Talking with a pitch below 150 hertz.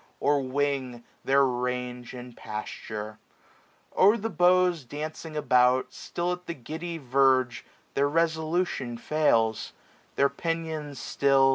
Yes: medium, 140 Hz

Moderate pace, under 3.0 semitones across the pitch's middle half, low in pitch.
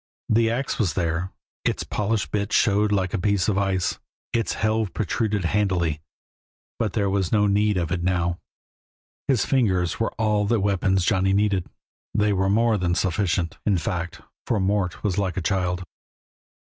Yes: average, 165 wpm; narrow, 2.6 semitones; low, 100 Hz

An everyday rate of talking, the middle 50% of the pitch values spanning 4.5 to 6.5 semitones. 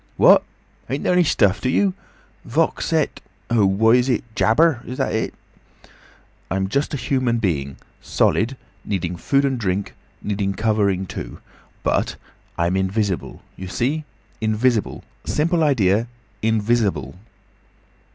No: slow, 115 wpm; average, 5.0 semitones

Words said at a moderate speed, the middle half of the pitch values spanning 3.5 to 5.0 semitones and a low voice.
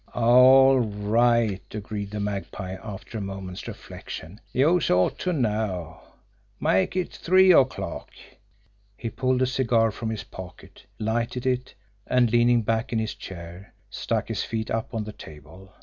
Yes: average, 150 wpm; average, 4.0 semitones; low, 110 Hz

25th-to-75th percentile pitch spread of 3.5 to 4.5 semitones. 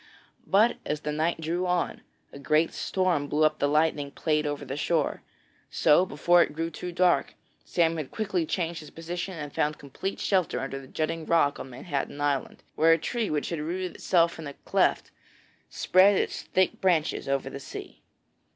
No: average, 3.1 semitones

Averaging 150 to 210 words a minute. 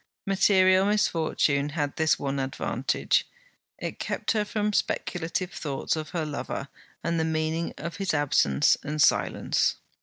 No: average, 140 wpm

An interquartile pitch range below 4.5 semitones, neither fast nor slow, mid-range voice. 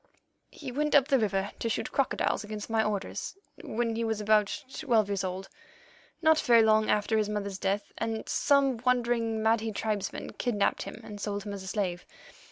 No: narrow, 2.6 semitones; average, 175 wpm; high, 220 Hz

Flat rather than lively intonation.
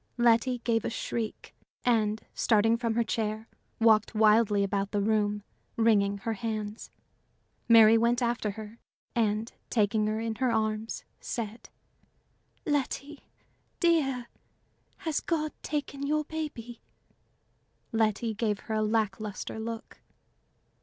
Yes: narrow, 1.9 semitones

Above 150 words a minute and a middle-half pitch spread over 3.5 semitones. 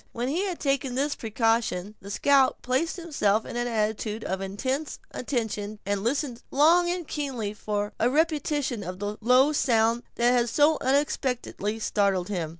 Yes: average, 160 wpm; average, 5.2 semitones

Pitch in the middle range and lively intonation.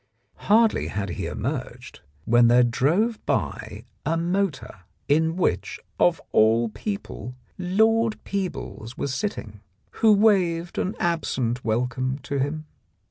Yes: medium, 160 Hz; wide, 8.5 semitones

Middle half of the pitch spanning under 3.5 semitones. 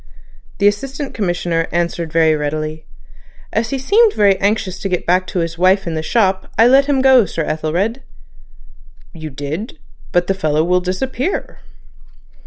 No: wide, 5.5 semitones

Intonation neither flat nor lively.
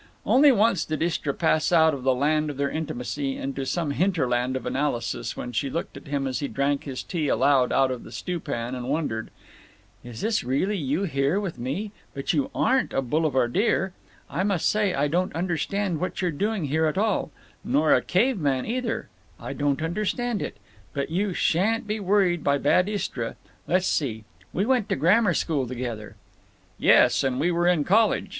No: wide, 6.0 semitones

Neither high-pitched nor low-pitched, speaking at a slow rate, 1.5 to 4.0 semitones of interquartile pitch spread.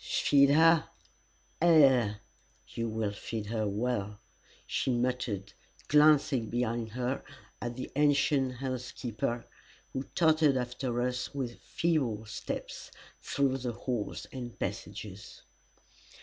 No: low, 125 Hz; slow, 105 wpm; average, 3.5 semitones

